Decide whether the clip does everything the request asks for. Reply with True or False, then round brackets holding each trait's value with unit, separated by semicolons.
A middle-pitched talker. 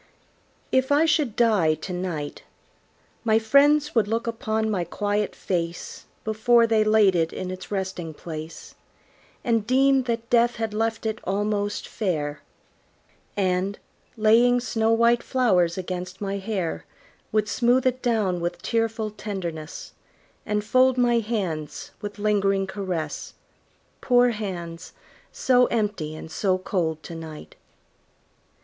False (210 Hz)